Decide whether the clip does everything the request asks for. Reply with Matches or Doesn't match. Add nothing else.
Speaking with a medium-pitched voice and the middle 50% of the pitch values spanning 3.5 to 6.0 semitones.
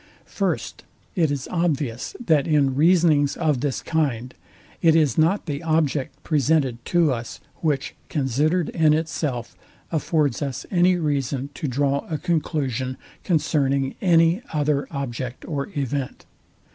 Doesn't match